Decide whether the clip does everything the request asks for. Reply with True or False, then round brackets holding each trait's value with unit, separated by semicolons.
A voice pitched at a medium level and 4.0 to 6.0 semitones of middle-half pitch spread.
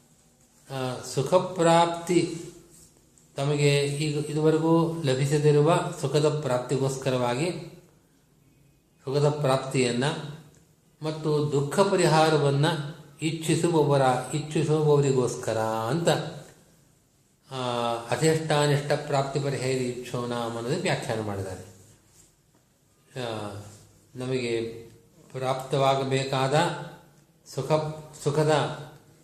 False (145 Hz; 3.3 semitones)